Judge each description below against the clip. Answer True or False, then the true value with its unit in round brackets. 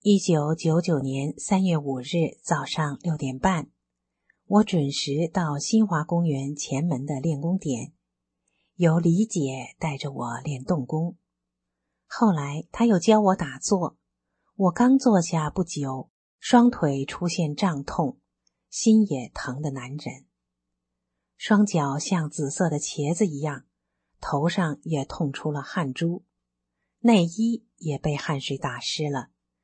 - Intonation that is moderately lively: True (4.9 semitones)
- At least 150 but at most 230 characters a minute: True (180 characters per minute)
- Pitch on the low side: False (150 Hz)